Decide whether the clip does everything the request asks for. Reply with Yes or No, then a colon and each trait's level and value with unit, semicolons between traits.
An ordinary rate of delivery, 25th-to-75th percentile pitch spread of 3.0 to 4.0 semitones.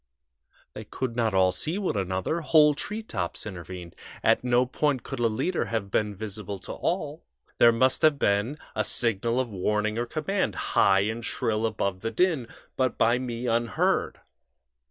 No: average, 165 wpm; average, 4.5 semitones